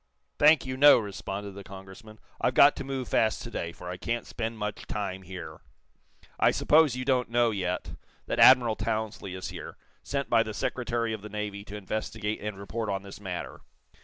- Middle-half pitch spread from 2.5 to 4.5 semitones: Yes, average, 3.2 semitones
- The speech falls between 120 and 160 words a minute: No, average, 190 wpm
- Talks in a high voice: No, low, 110 Hz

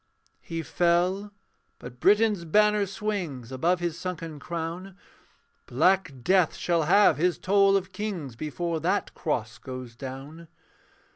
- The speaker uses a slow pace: Yes, slow, 125 wpm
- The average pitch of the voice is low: No, medium, 170 Hz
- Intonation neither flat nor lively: Yes, average, 4.5 semitones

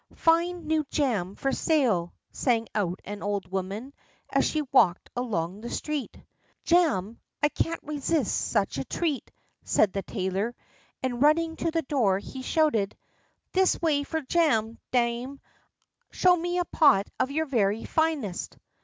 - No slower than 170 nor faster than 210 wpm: No, average, 145 wpm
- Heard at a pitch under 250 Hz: No, very high, 260 Hz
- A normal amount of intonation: No, wide, 7.6 semitones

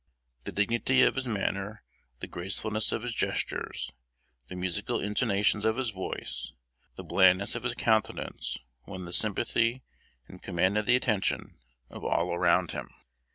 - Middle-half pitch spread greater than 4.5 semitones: No, average, 3.6 semitones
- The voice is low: Yes, low, 105 Hz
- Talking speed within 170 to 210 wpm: No, average, 145 wpm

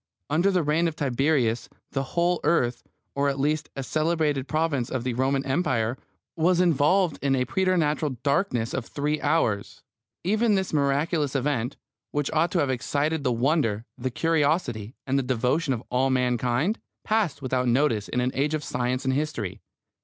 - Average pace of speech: Yes, average, 170 wpm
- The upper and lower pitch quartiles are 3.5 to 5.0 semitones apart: Yes, average, 3.9 semitones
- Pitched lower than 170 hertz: Yes, medium, 140 Hz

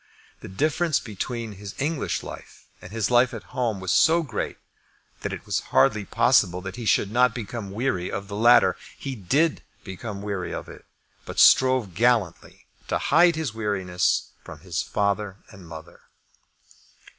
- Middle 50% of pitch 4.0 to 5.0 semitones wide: Yes, average, 4.6 semitones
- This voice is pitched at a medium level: No, low, 110 Hz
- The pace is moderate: Yes, average, 160 wpm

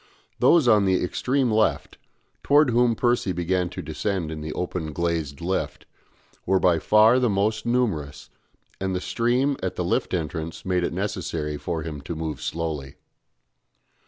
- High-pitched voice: No, very low, 90 Hz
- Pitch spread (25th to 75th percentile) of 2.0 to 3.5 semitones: No, average, 5.3 semitones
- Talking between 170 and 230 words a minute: No, average, 160 wpm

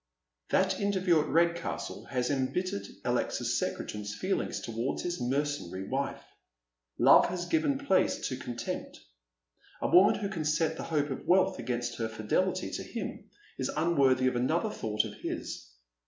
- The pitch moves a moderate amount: No, wide, 6.7 semitones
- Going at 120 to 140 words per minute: No, average, 150 wpm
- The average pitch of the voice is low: No, medium, 145 Hz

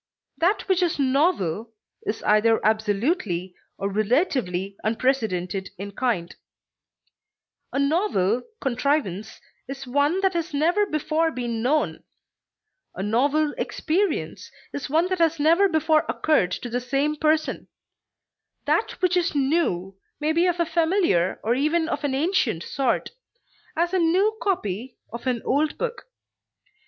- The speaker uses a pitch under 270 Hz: No, very high, 285 Hz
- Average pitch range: No, wide, 7.0 semitones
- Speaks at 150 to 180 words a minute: No, slow, 135 wpm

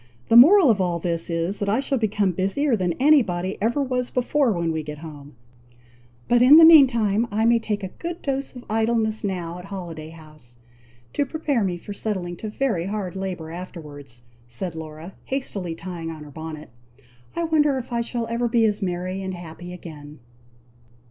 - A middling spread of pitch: No, wide, 6.1 semitones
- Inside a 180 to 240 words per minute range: Yes, average, 190 wpm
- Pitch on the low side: No, high, 195 Hz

